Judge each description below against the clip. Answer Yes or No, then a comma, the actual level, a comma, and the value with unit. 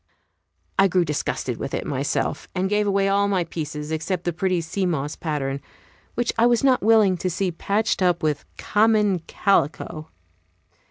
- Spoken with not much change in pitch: No, average, 4.1 semitones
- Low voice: No, medium, 185 Hz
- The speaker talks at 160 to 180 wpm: Yes, average, 165 wpm